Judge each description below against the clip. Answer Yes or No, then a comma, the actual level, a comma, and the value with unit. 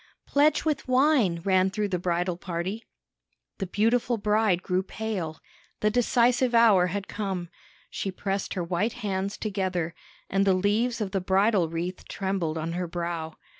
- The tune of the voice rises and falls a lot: No, average, 3.6 semitones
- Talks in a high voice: Yes, high, 195 Hz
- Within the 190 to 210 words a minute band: No, average, 155 wpm